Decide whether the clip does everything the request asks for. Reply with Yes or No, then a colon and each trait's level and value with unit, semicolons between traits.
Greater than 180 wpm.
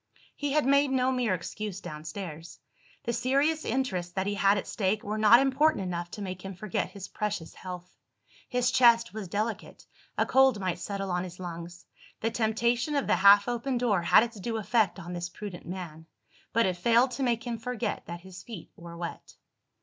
Yes: average, 195 wpm